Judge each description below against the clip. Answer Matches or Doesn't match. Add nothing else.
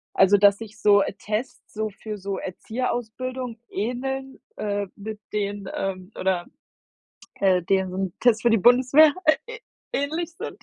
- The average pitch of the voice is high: Matches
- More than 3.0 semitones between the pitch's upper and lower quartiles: Matches